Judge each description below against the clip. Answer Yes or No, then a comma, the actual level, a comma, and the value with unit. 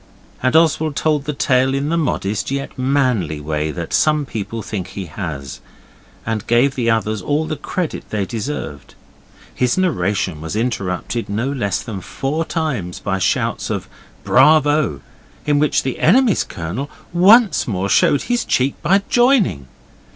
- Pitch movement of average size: No, wide, 7.5 semitones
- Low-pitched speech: Yes, low, 125 Hz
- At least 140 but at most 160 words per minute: Yes, average, 150 wpm